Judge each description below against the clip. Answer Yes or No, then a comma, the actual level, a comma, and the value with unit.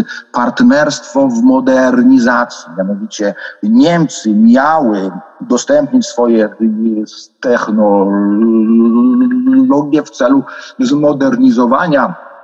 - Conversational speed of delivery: No, slow, 65 wpm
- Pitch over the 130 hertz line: Yes, medium, 140 Hz